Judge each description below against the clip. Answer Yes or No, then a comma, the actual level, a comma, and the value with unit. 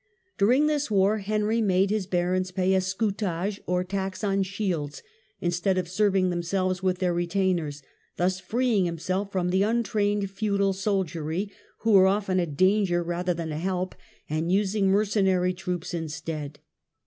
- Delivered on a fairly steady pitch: Yes, narrow, 2.3 semitones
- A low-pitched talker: No, high, 190 Hz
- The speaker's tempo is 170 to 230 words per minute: No, average, 150 wpm